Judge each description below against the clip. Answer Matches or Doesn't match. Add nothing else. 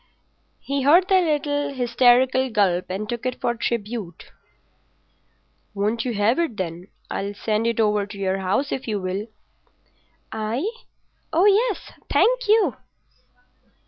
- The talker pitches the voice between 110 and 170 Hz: Doesn't match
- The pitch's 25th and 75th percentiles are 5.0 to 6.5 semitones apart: Matches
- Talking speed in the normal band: Doesn't match